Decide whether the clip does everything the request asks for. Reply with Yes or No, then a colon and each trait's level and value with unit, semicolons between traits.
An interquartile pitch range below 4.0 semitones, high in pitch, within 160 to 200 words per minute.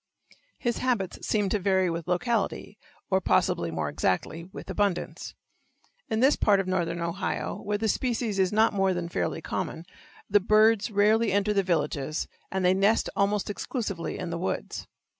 Yes: average, 3.3 semitones; high, 195 Hz; average, 165 wpm